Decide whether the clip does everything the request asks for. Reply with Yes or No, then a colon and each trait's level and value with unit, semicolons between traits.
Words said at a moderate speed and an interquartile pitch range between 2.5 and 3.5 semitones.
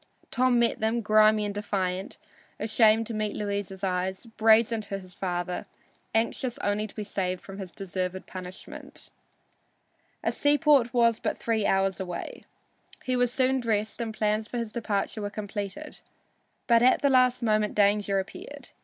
Yes: average, 155 wpm; average, 2.9 semitones